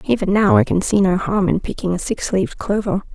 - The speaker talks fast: Yes, fast, 250 wpm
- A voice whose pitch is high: Yes, high, 200 Hz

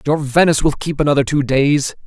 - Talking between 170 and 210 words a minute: Yes, fast, 205 wpm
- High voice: No, medium, 145 Hz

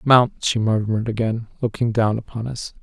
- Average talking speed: Yes, average, 170 wpm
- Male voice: Yes, male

